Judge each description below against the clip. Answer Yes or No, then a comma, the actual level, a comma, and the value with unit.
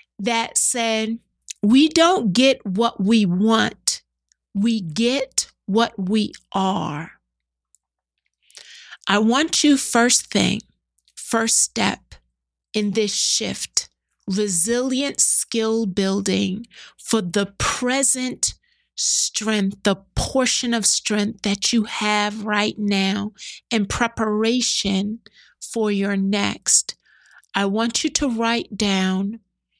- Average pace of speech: No, slow, 100 wpm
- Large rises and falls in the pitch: No, average, 2.9 semitones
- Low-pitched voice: No, high, 215 Hz